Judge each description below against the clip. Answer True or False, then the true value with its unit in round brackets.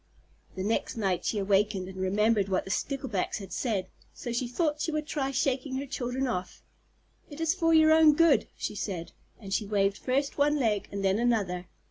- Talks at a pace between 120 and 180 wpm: False (195 wpm)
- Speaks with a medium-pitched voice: False (235 Hz)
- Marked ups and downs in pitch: True (6.2 semitones)